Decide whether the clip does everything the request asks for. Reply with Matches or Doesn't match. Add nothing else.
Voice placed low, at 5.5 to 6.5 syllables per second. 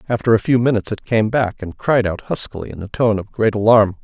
Matches